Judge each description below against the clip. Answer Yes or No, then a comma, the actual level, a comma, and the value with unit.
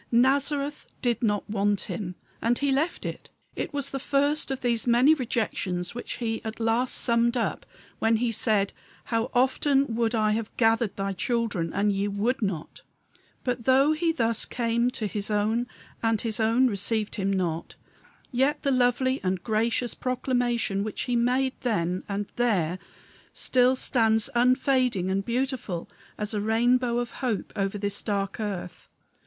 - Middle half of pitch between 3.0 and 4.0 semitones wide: Yes, average, 3.6 semitones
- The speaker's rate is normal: Yes, average, 160 wpm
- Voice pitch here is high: Yes, high, 230 Hz